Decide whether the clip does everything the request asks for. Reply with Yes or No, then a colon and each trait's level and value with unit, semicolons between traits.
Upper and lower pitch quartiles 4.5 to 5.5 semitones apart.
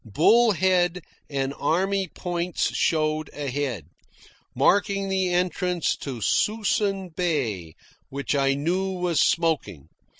Yes: average, 5.1 semitones